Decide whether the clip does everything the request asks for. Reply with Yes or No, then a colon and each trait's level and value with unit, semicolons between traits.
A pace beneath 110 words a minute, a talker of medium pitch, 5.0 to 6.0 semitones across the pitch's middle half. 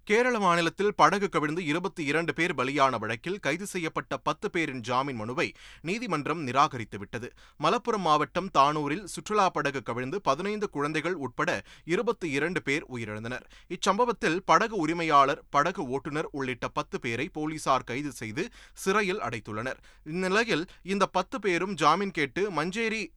No: fast, 130 wpm; medium, 155 Hz; wide, 5.5 semitones